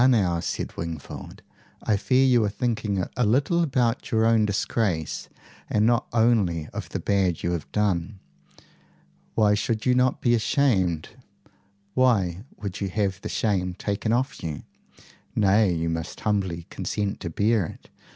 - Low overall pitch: Yes, low, 105 Hz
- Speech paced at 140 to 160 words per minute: Yes, average, 150 wpm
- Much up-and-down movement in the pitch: No, average, 4.4 semitones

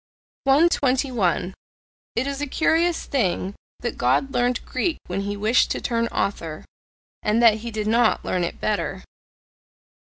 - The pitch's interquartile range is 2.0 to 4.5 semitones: No, average, 5.0 semitones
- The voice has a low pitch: No, high, 230 Hz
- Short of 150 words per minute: Yes, average, 140 wpm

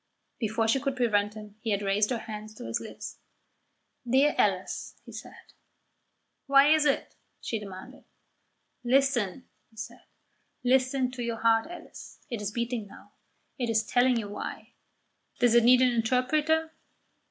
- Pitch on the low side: No, high, 235 Hz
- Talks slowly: No, average, 155 wpm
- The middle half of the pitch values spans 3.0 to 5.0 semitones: Yes, average, 3.3 semitones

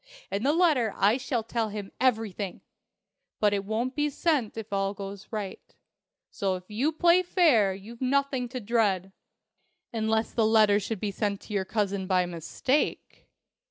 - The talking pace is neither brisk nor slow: Yes, average, 160 wpm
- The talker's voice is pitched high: Yes, high, 220 Hz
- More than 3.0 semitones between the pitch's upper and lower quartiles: Yes, average, 4.2 semitones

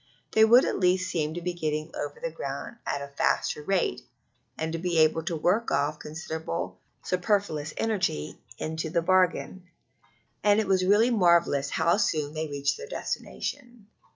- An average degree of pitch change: Yes, average, 4.2 semitones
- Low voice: No, medium, 170 Hz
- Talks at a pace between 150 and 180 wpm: Yes, average, 160 wpm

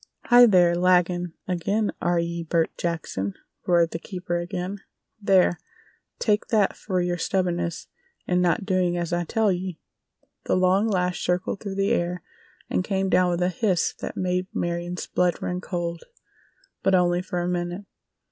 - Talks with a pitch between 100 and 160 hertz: No, medium, 180 Hz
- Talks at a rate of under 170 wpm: Yes, average, 155 wpm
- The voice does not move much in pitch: Yes, narrow, 1.5 semitones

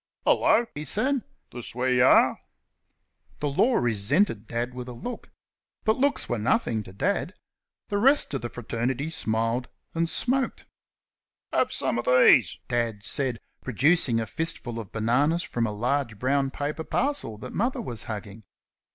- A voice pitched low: Yes, low, 125 Hz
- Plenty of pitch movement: Yes, wide, 6.5 semitones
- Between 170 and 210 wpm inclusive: No, average, 155 wpm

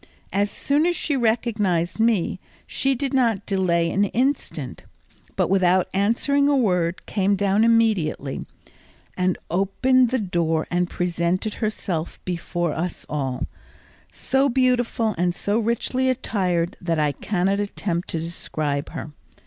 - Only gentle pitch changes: No, average, 5.3 semitones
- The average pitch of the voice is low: No, high, 195 Hz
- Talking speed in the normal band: No, slow, 130 wpm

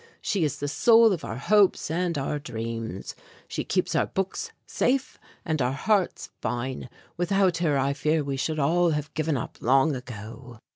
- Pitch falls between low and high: Yes, medium, 150 Hz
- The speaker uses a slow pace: No, average, 175 wpm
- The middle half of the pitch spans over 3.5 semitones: Yes, average, 5.1 semitones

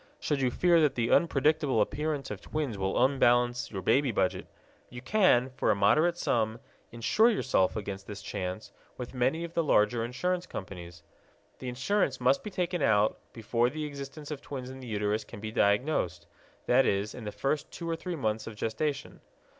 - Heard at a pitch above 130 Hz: No, low, 125 Hz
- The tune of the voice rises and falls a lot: Yes, wide, 5.9 semitones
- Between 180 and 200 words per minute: Yes, average, 185 wpm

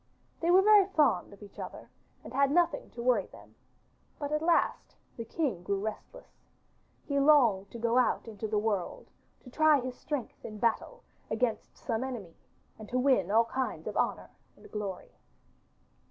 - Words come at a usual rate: Yes, average, 170 wpm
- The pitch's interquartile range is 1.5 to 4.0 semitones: No, wide, 5.5 semitones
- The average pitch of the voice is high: Yes, high, 245 Hz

